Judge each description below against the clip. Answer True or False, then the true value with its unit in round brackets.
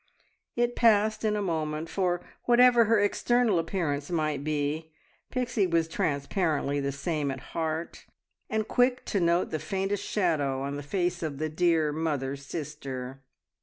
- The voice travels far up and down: True (5.7 semitones)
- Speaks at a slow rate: False (150 wpm)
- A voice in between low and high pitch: True (165 Hz)